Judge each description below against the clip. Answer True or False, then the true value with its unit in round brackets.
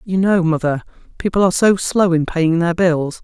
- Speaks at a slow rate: False (205 wpm)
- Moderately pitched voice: True (175 Hz)